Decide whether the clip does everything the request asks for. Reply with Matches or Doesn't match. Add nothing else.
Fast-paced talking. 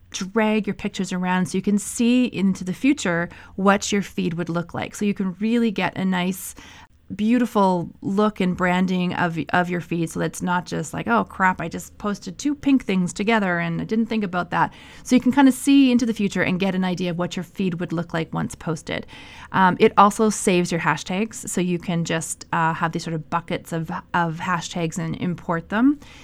Matches